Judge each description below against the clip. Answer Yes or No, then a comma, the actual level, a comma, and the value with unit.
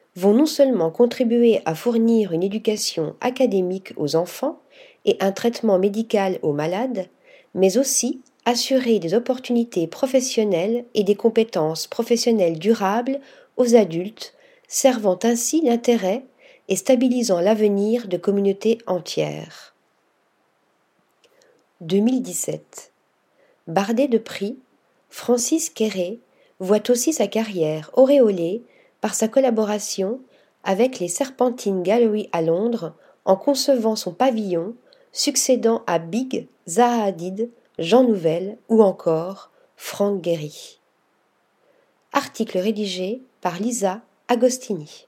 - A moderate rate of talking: No, slow, 105 wpm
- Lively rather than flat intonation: No, average, 4.8 semitones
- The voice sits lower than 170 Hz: No, high, 225 Hz